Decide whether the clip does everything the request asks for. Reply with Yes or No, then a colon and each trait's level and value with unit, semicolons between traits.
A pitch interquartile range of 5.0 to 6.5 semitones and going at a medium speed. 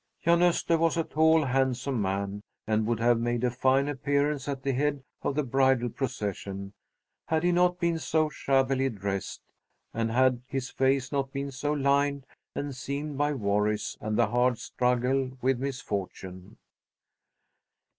No: average, 3.2 semitones; average, 155 wpm